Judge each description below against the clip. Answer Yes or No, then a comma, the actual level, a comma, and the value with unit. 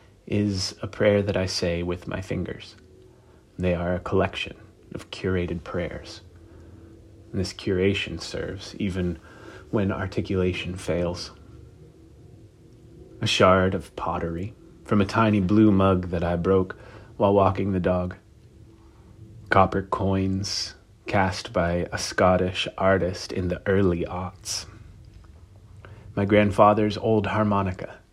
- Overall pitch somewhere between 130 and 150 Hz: No, very low, 95 Hz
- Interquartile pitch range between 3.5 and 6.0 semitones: No, narrow, 2.6 semitones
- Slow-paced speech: Yes, slow, 115 wpm